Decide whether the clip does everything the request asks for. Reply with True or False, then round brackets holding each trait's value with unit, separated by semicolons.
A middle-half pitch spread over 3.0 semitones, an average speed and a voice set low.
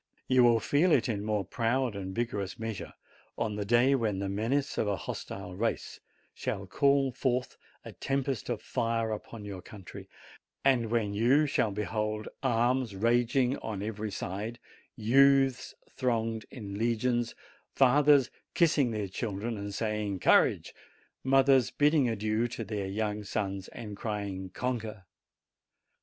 True (3.6 semitones; 145 wpm; 115 Hz)